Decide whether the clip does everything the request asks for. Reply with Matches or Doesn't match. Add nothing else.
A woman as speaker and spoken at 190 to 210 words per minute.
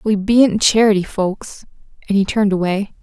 Doesn't match